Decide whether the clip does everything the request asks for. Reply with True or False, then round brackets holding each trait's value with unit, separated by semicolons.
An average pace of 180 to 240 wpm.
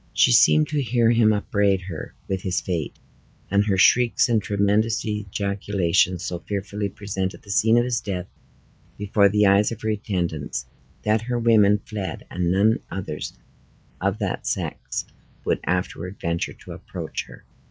False (155 wpm)